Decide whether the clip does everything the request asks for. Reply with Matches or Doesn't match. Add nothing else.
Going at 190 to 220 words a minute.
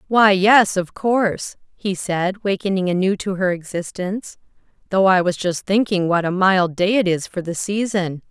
Doesn't match